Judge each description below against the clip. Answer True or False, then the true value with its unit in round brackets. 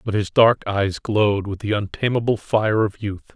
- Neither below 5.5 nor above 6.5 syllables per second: False (4.8 syllables/s)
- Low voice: True (105 Hz)